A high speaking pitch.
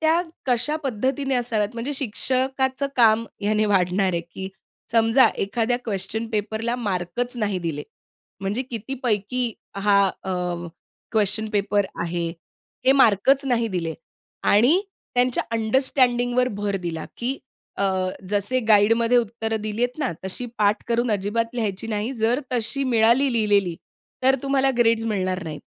Yes: high, 225 Hz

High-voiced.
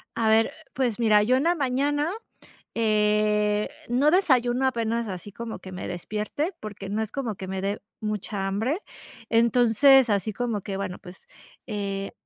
Yes: high, 220 Hz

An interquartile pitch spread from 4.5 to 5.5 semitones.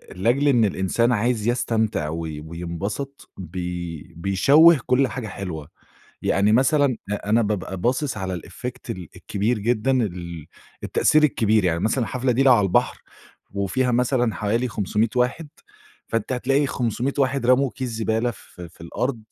Yes: average, 5.0 semitones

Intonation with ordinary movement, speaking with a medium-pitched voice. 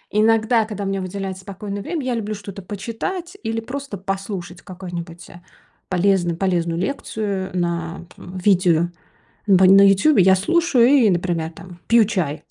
No: average, 3.6 semitones; high, 195 Hz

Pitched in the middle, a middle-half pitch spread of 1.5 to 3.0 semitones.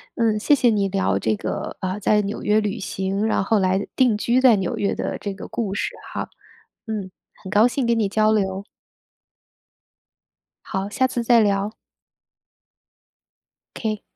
No: high, 210 Hz; narrow, 2.5 semitones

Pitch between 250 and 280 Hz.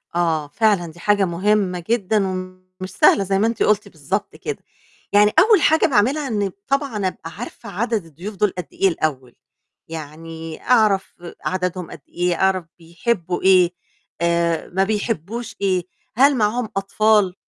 No: high, 190 Hz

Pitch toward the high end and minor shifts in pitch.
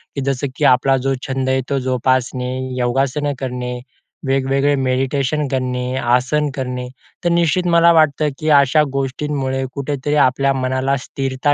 No: low, 135 Hz; narrow, 2.0 semitones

